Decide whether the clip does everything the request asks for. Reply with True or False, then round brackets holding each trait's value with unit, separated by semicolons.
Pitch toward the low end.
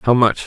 True (115 Hz)